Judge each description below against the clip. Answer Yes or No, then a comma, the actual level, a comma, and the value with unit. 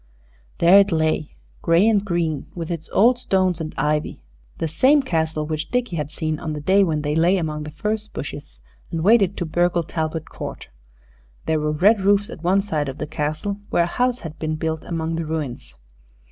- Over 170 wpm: Yes, average, 200 wpm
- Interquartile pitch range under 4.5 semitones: Yes, average, 3.9 semitones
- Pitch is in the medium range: Yes, medium, 165 Hz